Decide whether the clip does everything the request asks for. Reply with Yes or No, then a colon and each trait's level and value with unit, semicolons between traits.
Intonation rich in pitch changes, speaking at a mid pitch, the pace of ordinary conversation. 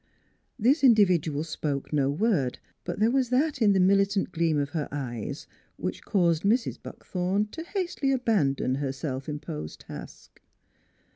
Yes: wide, 7.8 semitones; medium, 180 Hz; average, 150 wpm